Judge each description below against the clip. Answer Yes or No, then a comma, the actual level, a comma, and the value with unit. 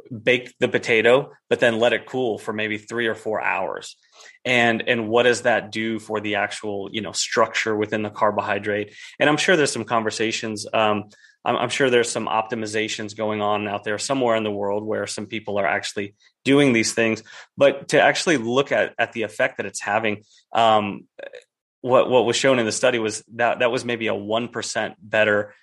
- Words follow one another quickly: Yes, fast, 210 wpm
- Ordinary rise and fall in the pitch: No, narrow, 2.1 semitones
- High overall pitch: No, low, 110 Hz